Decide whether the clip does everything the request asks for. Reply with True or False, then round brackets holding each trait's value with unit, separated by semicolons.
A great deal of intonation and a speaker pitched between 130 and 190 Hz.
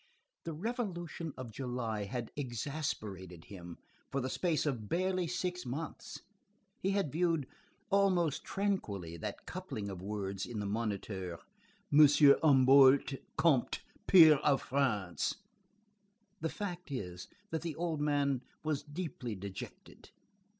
True (7.6 semitones; 140 Hz)